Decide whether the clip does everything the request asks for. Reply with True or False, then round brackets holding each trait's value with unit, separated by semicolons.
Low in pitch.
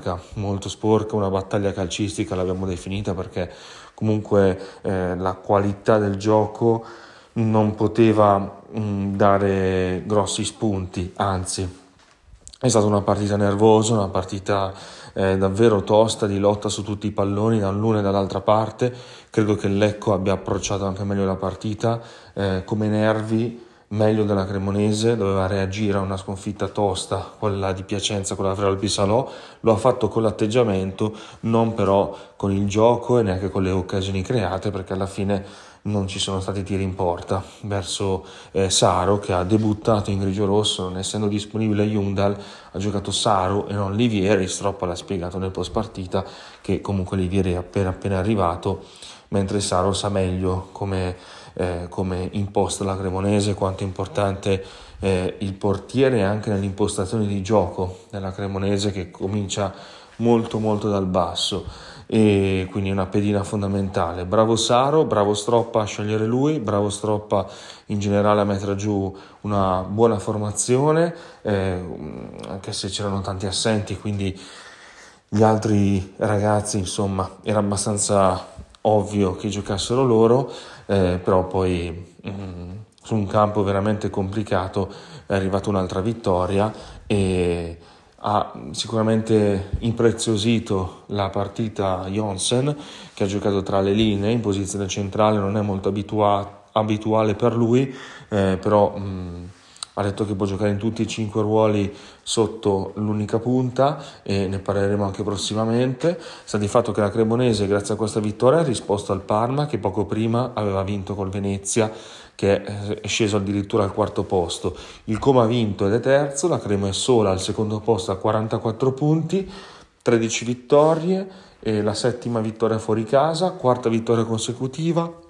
True (100 Hz)